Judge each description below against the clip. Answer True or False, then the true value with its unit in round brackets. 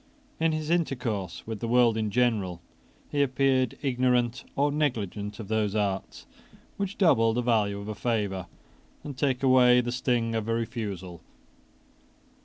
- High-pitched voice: False (115 Hz)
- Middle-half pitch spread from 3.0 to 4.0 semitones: True (3.6 semitones)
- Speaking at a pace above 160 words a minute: False (150 wpm)